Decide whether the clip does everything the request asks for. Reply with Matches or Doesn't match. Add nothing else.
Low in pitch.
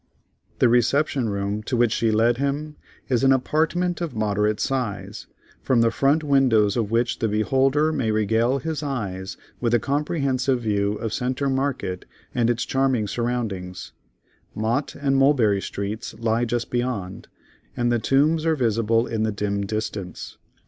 Matches